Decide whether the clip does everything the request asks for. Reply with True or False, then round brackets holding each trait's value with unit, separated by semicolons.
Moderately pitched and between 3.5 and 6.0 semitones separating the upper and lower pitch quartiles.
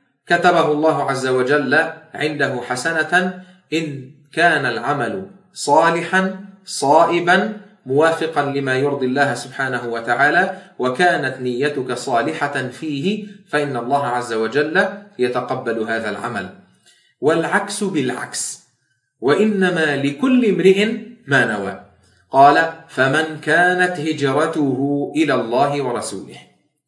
True (155 Hz; 5.4 semitones)